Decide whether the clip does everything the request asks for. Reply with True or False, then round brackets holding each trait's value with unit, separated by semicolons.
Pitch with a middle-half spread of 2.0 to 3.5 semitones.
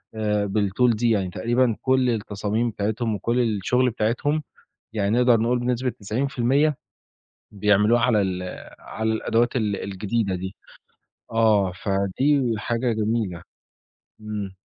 True (3.0 semitones)